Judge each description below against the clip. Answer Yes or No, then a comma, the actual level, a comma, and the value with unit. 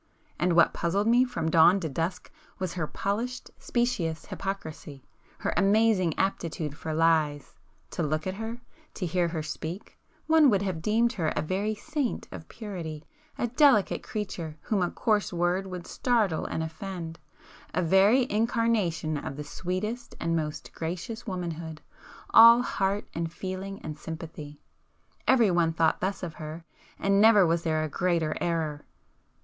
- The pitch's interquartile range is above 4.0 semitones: Yes, average, 4.7 semitones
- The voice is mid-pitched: Yes, medium, 180 Hz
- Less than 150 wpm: Yes, average, 140 wpm